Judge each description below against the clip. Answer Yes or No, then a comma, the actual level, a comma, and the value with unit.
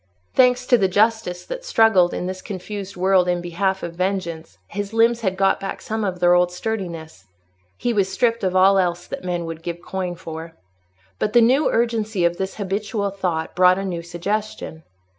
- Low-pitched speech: No, high, 190 Hz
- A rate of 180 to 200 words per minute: Yes, average, 190 wpm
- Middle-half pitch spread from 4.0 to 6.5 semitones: No, average, 3.3 semitones